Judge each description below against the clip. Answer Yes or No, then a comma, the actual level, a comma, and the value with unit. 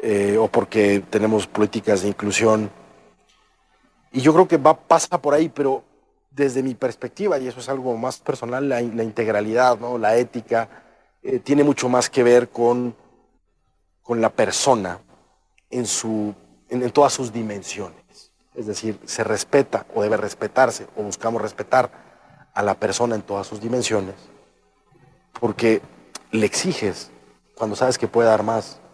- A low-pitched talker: Yes, low, 115 Hz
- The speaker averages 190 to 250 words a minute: No, average, 155 wpm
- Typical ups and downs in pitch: Yes, average, 3.4 semitones